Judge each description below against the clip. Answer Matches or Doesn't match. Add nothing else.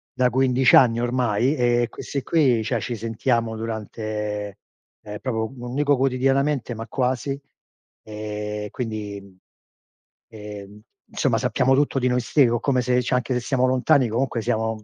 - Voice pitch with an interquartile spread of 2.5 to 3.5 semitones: Matches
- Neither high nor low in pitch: Doesn't match